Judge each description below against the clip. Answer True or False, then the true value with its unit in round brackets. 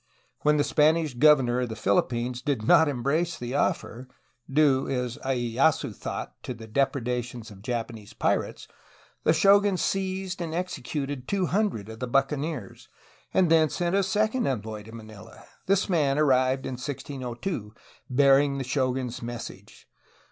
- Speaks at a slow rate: False (145 wpm)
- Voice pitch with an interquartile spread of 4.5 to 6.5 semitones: True (4.8 semitones)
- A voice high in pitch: False (135 Hz)